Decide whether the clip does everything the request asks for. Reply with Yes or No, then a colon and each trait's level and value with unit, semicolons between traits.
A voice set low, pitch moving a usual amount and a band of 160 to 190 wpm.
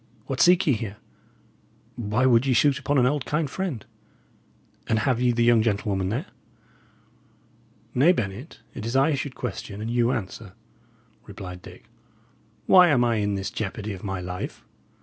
Yes: low, 120 Hz; average, 4.8 semitones; average, 165 wpm